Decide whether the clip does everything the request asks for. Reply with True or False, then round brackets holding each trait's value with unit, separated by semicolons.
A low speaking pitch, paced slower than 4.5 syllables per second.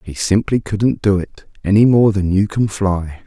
True (100 Hz; 4.3 syllables/s)